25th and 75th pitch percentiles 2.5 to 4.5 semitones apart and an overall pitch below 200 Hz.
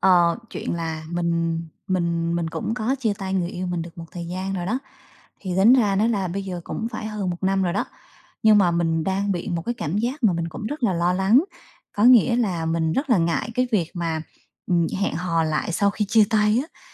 Yes: average, 3.9 semitones; medium, 185 Hz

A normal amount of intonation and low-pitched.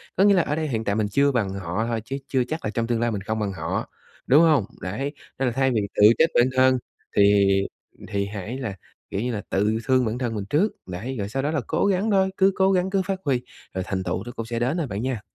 No: wide, 5.8 semitones; low, 120 Hz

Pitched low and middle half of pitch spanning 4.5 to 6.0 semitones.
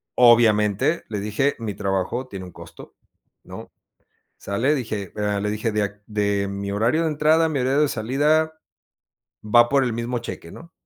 Yes: low, 115 Hz; average, 5.3 semitones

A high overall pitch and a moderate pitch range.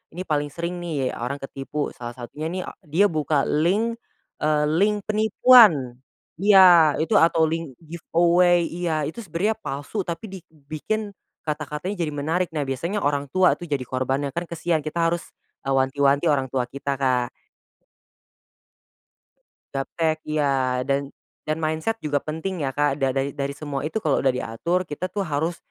No: medium, 155 Hz; average, 4.0 semitones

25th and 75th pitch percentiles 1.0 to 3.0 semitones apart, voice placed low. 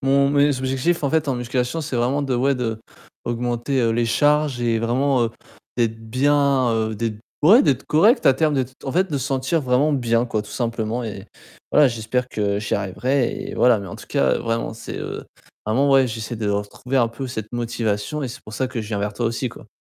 No: average, 3.4 semitones; low, 125 Hz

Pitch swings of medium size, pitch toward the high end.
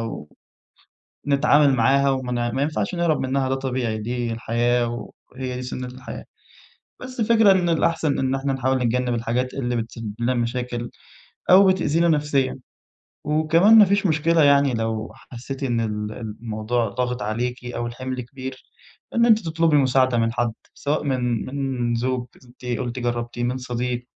No: average, 3.1 semitones; low, 125 Hz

